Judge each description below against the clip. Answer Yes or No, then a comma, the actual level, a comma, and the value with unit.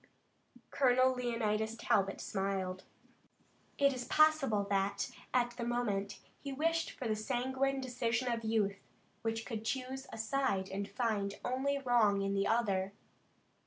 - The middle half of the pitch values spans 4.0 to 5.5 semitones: Yes, average, 4.4 semitones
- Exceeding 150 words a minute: No, slow, 135 wpm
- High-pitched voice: Yes, high, 230 Hz